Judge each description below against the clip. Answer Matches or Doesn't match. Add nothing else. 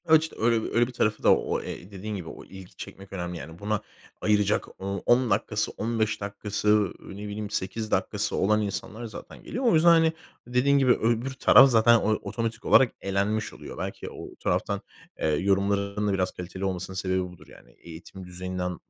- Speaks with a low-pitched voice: Matches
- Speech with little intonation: Doesn't match